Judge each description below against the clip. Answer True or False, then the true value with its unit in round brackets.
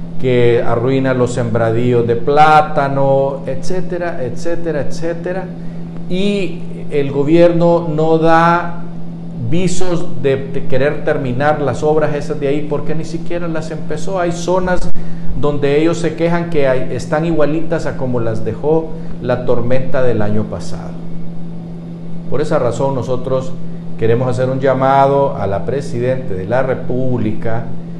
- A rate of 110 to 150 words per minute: True (135 wpm)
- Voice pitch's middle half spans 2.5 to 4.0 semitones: False (4.5 semitones)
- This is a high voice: False (155 Hz)